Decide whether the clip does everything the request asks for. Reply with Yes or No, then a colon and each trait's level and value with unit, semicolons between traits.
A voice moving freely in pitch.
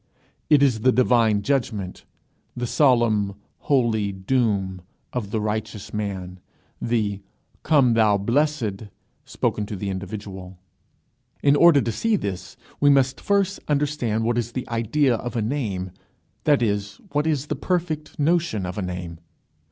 Yes: wide, 5.7 semitones